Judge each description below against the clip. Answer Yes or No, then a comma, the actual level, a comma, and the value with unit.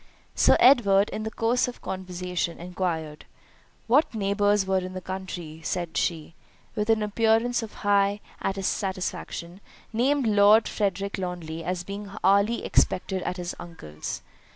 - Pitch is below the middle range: No, high, 195 Hz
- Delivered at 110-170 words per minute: Yes, slow, 135 wpm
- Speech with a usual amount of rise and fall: Yes, average, 3.0 semitones